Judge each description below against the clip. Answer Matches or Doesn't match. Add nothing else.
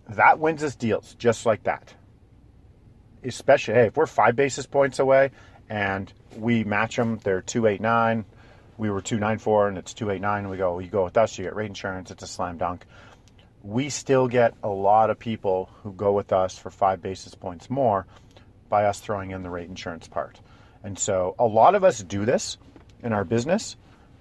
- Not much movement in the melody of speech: Doesn't match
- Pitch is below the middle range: Matches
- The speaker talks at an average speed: Matches